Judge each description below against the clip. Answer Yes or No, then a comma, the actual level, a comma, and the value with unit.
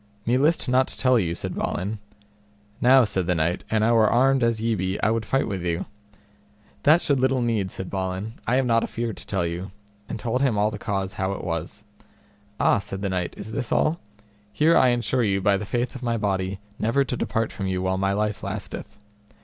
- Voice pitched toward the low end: Yes, low, 110 Hz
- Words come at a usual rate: No, fast, 220 wpm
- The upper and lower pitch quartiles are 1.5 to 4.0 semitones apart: No, average, 4.4 semitones